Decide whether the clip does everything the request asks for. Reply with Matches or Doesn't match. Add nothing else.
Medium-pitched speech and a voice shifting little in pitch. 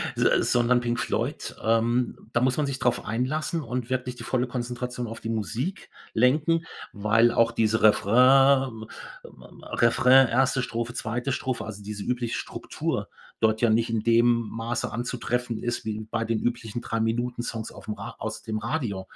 Doesn't match